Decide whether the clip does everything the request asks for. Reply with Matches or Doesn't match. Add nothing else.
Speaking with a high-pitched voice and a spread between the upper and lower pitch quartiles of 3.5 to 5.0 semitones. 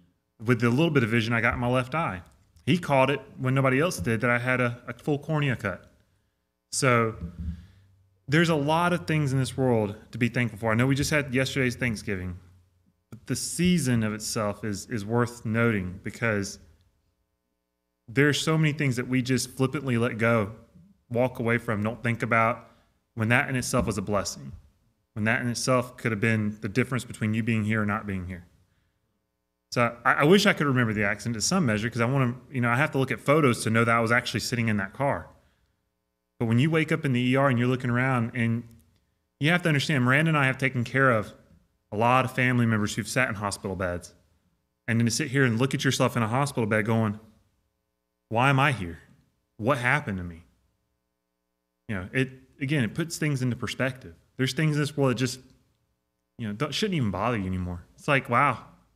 Doesn't match